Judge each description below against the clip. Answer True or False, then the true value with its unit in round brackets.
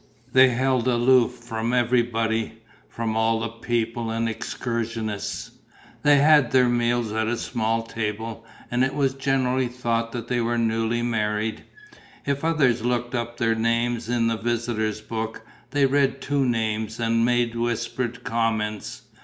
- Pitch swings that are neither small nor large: False (1.6 semitones)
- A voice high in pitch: False (115 Hz)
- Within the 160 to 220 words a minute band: False (145 wpm)